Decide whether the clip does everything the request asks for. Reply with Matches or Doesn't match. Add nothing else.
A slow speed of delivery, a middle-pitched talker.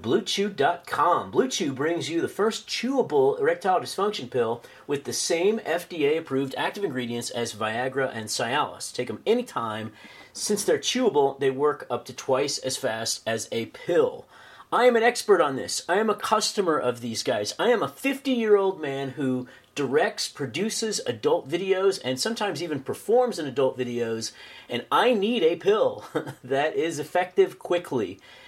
Doesn't match